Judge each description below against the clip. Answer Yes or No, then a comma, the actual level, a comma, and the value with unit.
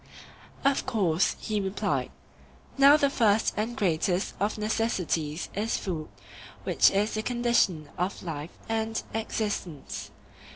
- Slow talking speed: Yes, slow, 120 wpm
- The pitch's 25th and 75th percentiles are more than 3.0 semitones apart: Yes, average, 4.1 semitones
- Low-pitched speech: No, high, 210 Hz